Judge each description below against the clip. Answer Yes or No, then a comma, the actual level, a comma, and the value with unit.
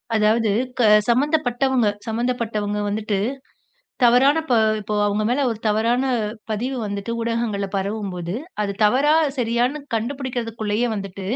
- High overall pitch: Yes, high, 230 Hz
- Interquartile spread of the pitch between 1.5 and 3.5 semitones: Yes, average, 3.0 semitones